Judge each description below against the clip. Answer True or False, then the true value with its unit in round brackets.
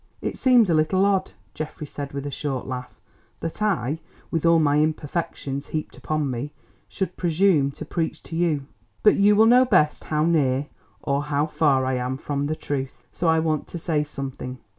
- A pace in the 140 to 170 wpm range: False (185 wpm)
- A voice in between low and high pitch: True (155 Hz)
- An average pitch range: True (3.4 semitones)